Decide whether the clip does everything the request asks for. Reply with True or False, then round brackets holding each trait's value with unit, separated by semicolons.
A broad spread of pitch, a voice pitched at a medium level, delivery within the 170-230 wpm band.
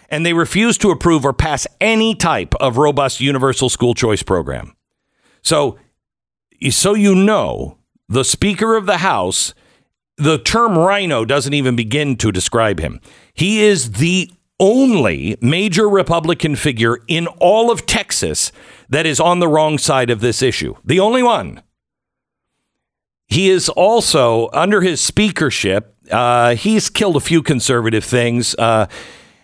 False (7.7 semitones; 155 Hz; 145 wpm)